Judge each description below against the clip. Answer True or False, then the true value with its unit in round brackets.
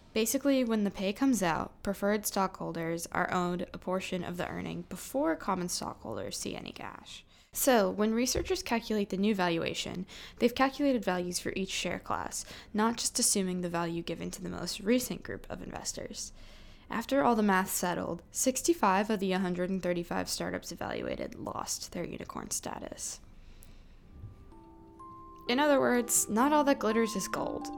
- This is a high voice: True (205 Hz)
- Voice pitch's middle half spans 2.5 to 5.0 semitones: False (5.6 semitones)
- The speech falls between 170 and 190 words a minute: False (155 wpm)